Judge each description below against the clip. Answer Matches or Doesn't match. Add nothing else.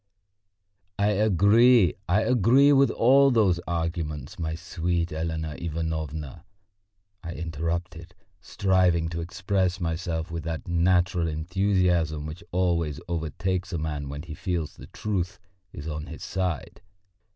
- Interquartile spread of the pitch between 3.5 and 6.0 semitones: Doesn't match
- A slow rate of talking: Matches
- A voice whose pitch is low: Matches